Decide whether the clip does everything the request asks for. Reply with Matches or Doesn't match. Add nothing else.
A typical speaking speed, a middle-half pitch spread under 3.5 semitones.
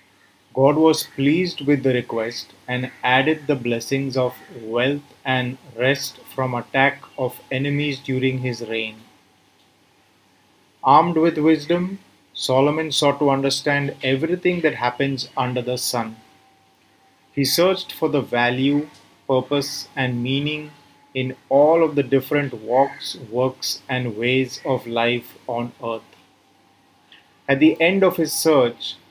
Matches